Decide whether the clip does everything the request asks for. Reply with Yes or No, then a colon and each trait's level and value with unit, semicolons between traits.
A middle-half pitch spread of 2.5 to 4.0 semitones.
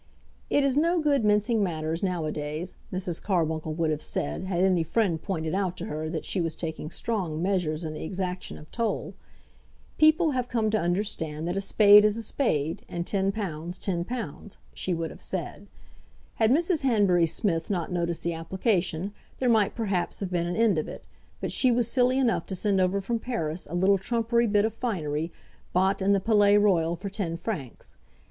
No: average, 4.7 semitones